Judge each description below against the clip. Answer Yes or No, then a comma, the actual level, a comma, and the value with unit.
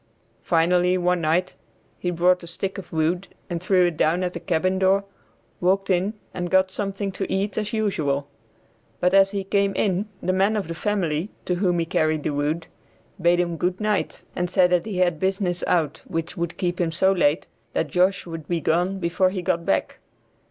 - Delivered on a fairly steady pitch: Yes, narrow, 2.3 semitones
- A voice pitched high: No, medium, 180 Hz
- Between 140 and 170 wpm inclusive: No, average, 200 wpm